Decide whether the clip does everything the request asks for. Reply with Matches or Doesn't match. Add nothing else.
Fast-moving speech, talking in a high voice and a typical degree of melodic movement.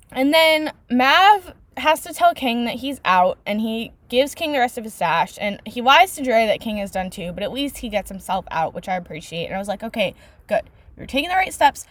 Doesn't match